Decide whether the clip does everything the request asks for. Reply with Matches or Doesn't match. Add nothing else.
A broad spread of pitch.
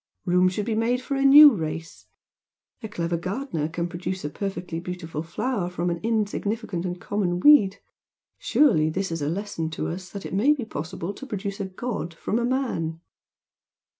Doesn't match